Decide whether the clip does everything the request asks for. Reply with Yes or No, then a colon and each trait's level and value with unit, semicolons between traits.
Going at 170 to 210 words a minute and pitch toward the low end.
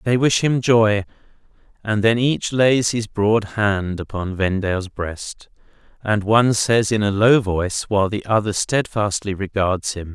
No: average, 160 wpm; low, 105 Hz